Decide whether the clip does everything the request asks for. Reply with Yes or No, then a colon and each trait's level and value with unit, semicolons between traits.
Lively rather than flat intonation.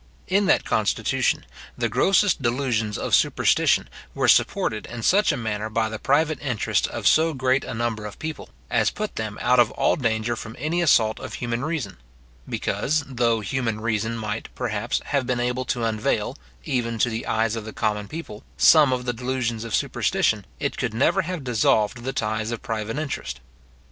No: average, 3.5 semitones